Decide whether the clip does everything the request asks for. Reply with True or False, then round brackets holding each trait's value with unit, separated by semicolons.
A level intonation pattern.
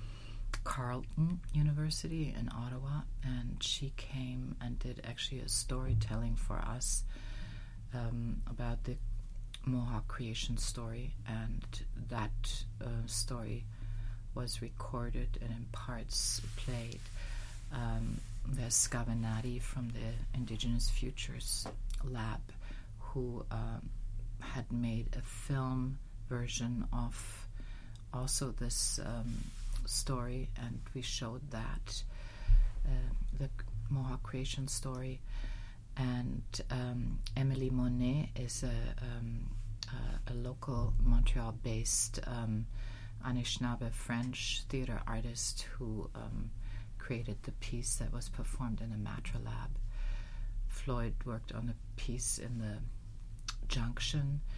True (2.1 semitones)